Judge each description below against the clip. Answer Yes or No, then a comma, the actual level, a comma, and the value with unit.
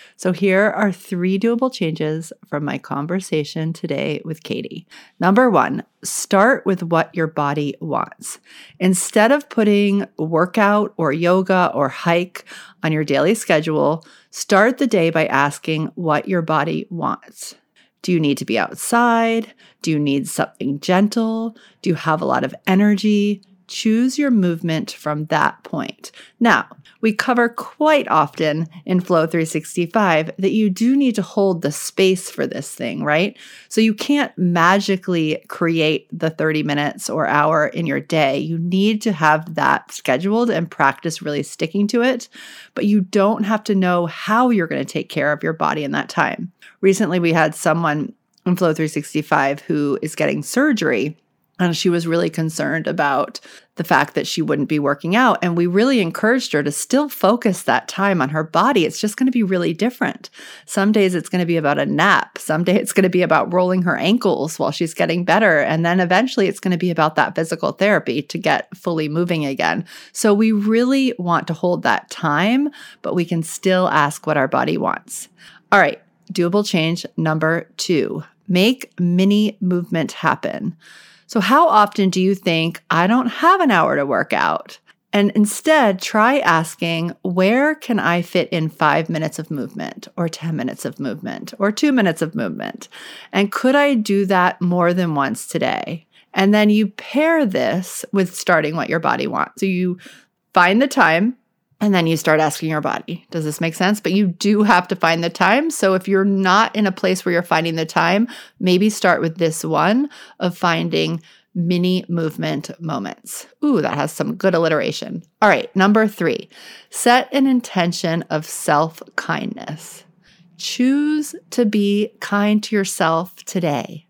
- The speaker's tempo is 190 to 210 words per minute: No, average, 175 wpm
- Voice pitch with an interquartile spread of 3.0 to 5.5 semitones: Yes, average, 4.5 semitones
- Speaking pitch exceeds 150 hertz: Yes, medium, 185 Hz